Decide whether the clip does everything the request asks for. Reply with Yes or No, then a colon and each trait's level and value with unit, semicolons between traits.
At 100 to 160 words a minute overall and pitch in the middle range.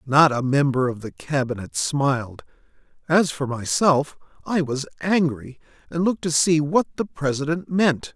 Yes: average, 155 wpm; medium, 150 Hz